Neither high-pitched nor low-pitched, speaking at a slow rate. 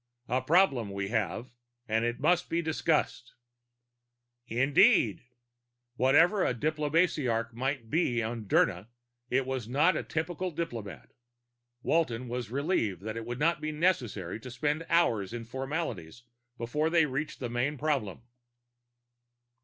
No: low, 130 Hz; slow, 130 wpm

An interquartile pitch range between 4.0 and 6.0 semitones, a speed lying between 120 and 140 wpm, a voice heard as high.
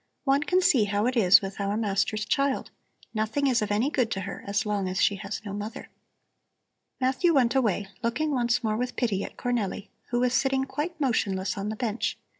No: average, 4.5 semitones; fast, 205 wpm; high, 225 Hz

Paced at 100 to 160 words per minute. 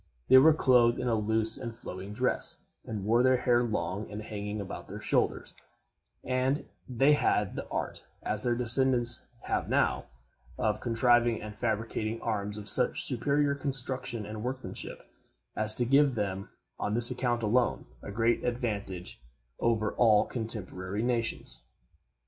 Yes: average, 150 wpm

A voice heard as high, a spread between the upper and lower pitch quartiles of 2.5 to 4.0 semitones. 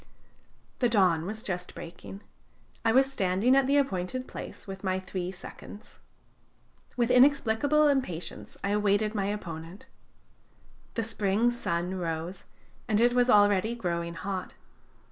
No: high, 205 Hz; average, 4.8 semitones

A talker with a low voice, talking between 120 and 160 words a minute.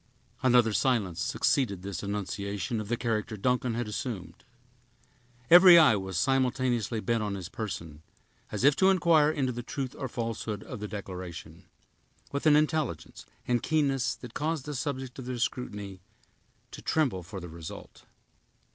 Yes: low, 115 Hz; average, 155 wpm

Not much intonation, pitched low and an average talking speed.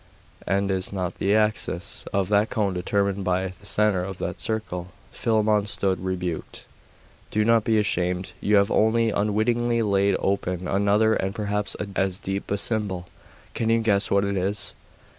Yes: narrow, 2.2 semitones; low, 100 Hz; average, 160 wpm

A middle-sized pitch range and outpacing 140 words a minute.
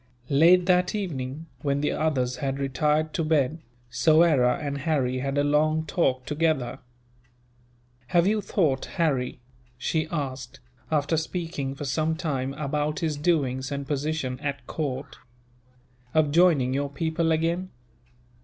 No: average, 3.0 semitones; slow, 135 wpm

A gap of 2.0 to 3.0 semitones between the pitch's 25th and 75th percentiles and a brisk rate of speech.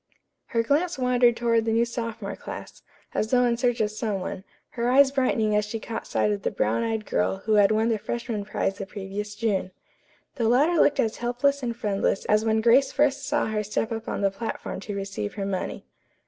Yes: average, 2.7 semitones; fast, 215 wpm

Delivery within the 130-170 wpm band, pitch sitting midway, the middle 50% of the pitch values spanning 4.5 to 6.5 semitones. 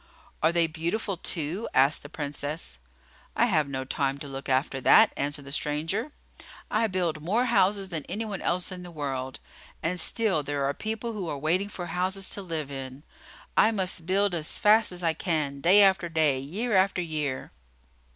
No: average, 185 wpm; medium, 165 Hz; average, 4.9 semitones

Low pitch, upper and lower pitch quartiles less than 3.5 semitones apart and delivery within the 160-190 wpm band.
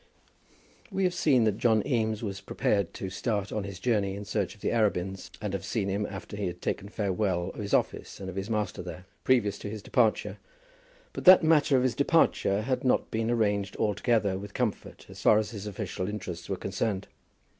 No: low, 105 Hz; average, 2.7 semitones; fast, 205 wpm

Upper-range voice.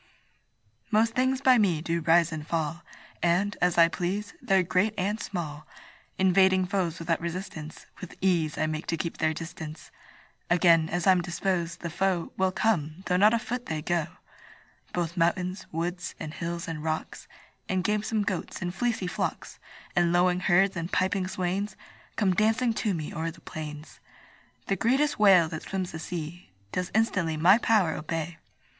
No: medium, 175 Hz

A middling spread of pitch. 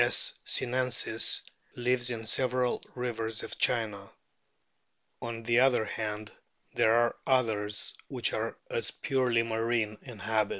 No: narrow, 2.1 semitones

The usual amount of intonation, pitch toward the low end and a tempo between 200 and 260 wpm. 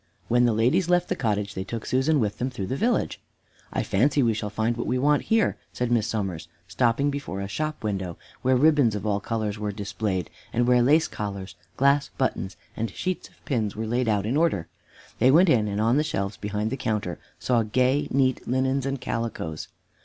Yes: average, 4.6 semitones; low, 115 Hz; fast, 205 wpm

